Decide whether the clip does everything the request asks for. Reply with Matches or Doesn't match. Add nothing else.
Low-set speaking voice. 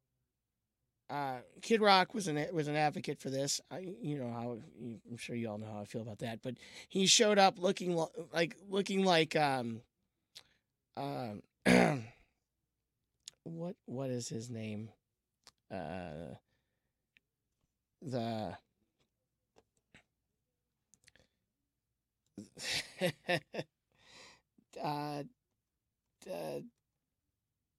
Matches